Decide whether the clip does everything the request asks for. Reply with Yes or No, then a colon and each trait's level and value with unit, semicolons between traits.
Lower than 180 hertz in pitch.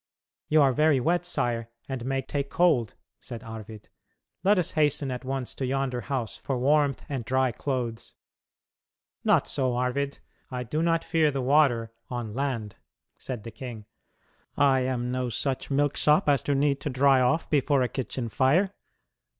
Yes: low, 135 Hz